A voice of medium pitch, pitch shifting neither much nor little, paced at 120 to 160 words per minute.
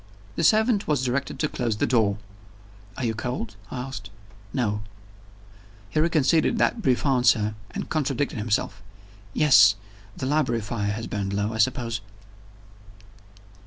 No: low, 120 Hz; average, 4.8 semitones; slow, 135 wpm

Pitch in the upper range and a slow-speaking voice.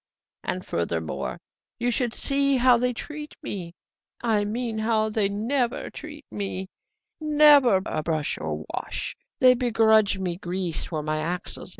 No: high, 220 Hz; average, 150 wpm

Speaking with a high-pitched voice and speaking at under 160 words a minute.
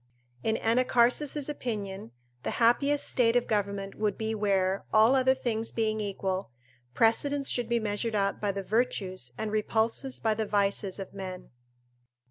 Yes: high, 220 Hz; average, 150 wpm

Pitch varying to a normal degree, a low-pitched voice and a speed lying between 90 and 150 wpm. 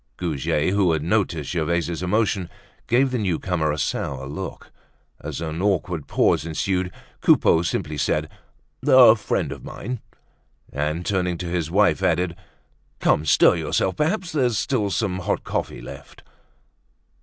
Yes: average, 4.5 semitones; very low, 90 Hz; average, 140 wpm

